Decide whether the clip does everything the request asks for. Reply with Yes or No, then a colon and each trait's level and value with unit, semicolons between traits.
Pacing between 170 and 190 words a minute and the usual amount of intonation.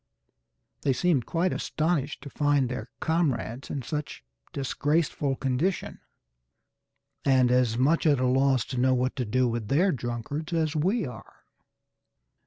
No: average, 140 wpm; average, 3.6 semitones